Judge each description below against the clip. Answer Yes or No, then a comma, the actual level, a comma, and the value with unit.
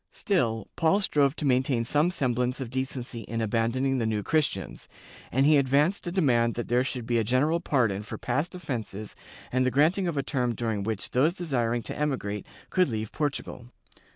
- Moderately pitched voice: No, low, 130 Hz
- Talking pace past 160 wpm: Yes, average, 185 wpm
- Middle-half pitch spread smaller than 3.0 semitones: No, average, 4.2 semitones